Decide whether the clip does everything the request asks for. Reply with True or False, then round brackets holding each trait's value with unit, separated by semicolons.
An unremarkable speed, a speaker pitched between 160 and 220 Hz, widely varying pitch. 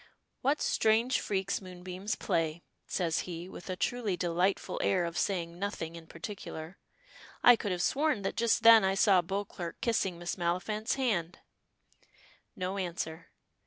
False (145 wpm; 185 Hz; 3.5 semitones)